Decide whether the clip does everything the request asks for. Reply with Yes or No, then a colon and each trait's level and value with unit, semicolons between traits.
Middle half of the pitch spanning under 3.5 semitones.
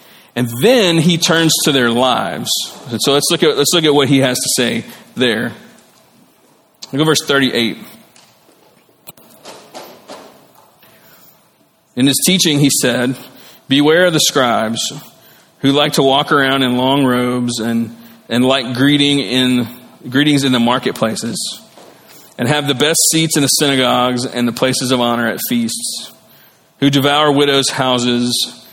Yes: average, 3.0 semitones